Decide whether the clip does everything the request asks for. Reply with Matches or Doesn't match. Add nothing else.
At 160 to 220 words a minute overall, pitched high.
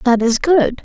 Matches